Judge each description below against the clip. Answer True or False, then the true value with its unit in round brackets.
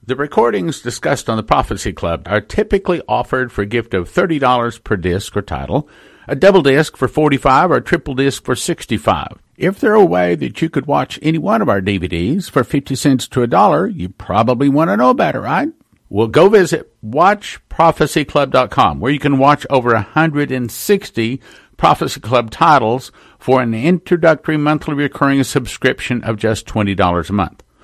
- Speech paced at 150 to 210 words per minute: True (175 wpm)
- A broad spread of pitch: True (5.8 semitones)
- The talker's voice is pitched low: True (130 Hz)